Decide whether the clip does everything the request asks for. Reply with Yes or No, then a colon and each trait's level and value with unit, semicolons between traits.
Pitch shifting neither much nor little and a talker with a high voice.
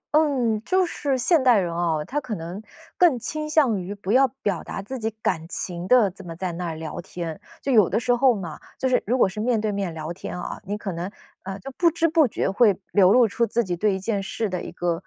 No: wide, 6.0 semitones; high, 210 Hz